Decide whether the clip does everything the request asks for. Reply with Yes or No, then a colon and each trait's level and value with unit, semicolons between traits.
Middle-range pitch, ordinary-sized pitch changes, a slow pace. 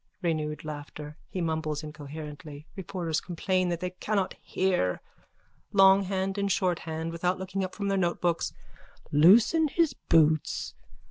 Yes: medium, 175 Hz; average, 3.7 semitones; slow, 130 wpm